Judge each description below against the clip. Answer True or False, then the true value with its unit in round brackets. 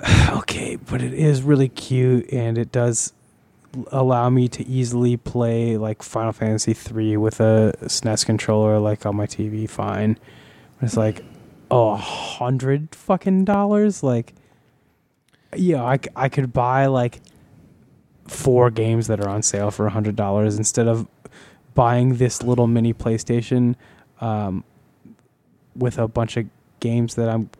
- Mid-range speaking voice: False (120 Hz)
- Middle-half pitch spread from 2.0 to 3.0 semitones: True (2.7 semitones)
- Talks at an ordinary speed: True (145 wpm)